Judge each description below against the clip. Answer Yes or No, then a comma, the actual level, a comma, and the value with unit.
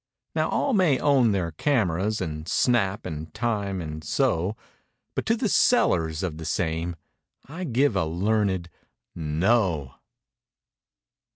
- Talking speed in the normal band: No, slow, 120 wpm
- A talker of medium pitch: No, very low, 95 Hz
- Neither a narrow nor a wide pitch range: No, wide, 6.6 semitones